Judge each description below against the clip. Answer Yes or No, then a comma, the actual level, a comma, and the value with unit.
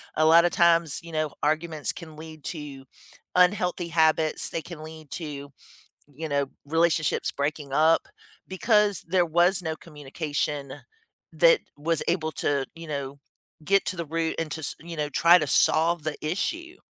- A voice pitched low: No, medium, 160 Hz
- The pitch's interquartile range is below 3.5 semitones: Yes, narrow, 2.4 semitones